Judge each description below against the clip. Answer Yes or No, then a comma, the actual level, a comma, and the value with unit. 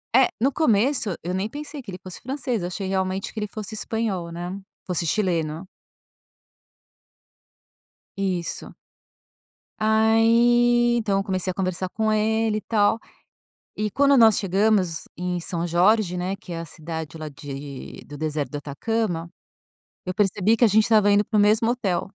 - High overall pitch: Yes, high, 195 Hz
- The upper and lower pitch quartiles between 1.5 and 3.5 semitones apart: No, average, 4.0 semitones